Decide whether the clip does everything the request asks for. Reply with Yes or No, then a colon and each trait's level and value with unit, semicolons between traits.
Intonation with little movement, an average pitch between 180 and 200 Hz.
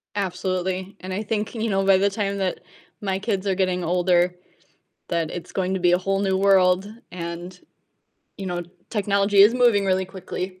Yes: narrow, 1.6 semitones; high, 190 Hz